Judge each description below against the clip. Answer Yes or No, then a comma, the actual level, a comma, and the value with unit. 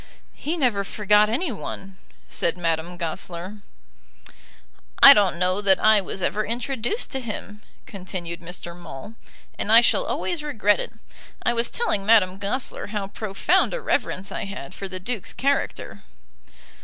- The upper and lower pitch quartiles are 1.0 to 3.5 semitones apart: No, average, 4.1 semitones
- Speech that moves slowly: No, average, 150 wpm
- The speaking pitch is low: No, high, 205 Hz